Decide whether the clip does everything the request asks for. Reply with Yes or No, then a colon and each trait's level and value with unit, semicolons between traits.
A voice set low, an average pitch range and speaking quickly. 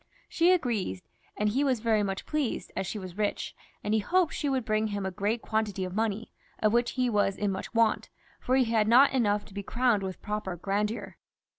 No: high, 215 Hz; average, 3.0 semitones; fast, 215 wpm